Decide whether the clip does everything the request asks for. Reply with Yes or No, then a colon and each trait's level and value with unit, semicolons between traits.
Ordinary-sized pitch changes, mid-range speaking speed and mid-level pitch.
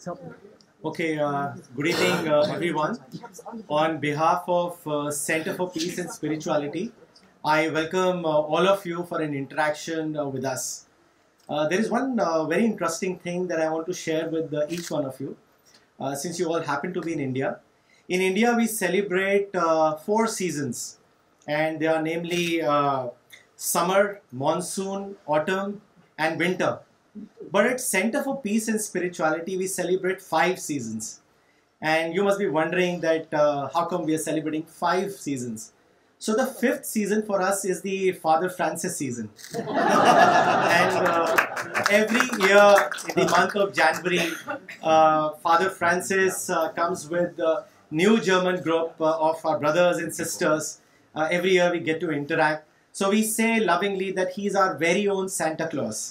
Yes: average, 3.3 semitones; average, 125 wpm; medium, 170 Hz